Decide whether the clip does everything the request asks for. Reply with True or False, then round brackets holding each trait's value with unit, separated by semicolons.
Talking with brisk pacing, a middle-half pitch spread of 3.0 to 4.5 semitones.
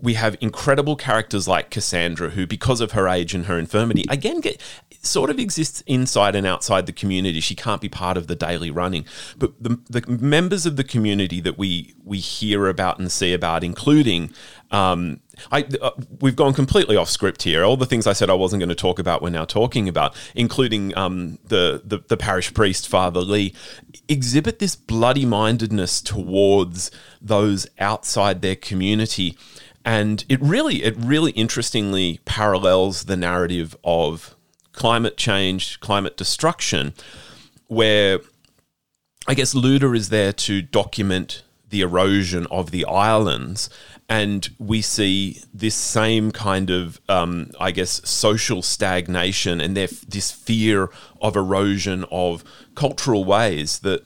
False (155 wpm; 3.9 semitones)